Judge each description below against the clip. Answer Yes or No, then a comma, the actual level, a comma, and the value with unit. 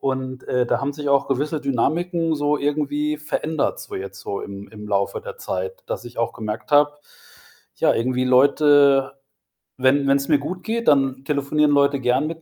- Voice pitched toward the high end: No, medium, 140 Hz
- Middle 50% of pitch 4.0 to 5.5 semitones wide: No, average, 2.8 semitones